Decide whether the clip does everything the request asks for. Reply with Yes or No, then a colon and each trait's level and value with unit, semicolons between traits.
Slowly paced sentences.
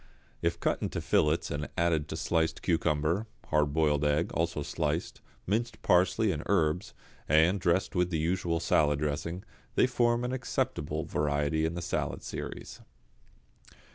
No: average, 145 wpm